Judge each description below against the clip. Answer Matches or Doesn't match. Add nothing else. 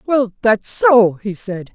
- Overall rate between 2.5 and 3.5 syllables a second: Matches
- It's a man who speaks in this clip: Doesn't match